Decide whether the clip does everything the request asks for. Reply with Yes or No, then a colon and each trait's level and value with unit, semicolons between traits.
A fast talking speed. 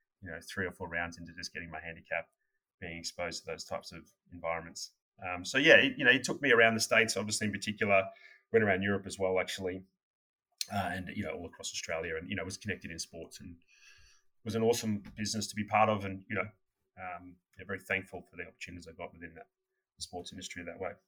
Yes: fast, 230 wpm